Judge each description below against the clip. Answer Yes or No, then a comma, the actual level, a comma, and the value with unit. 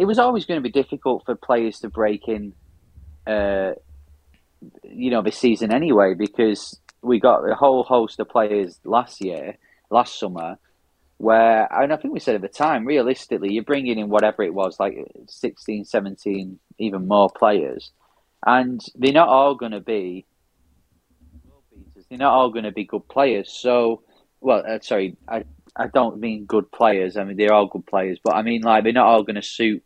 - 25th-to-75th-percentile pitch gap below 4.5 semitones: Yes, average, 3.7 semitones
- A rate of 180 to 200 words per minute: Yes, average, 185 wpm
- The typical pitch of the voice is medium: No, low, 105 Hz